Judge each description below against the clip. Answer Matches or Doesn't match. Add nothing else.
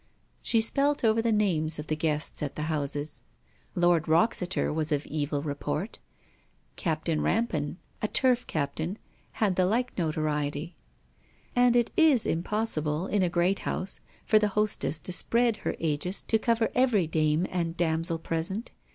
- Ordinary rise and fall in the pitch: Doesn't match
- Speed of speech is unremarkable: Matches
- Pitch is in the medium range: Matches